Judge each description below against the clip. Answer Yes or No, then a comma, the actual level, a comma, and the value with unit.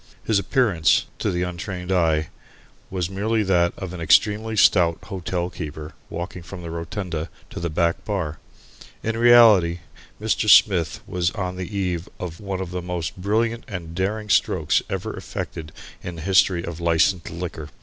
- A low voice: Yes, very low, 90 Hz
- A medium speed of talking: Yes, average, 160 wpm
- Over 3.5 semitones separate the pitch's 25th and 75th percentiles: No, average, 3.0 semitones